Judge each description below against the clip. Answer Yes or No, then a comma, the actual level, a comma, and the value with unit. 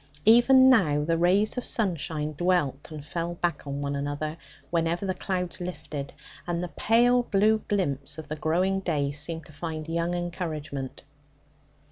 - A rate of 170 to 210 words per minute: No, average, 155 wpm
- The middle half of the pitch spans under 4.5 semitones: Yes, average, 3.9 semitones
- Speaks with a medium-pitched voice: Yes, medium, 170 Hz